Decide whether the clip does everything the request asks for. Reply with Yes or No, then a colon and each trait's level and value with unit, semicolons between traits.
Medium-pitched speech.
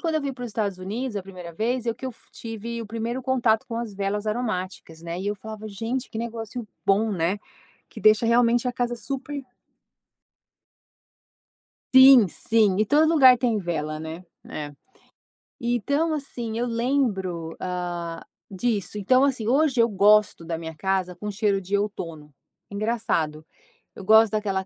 No: high, 215 Hz